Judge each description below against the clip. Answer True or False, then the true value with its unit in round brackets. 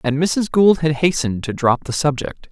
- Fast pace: True (215 wpm)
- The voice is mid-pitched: True (150 Hz)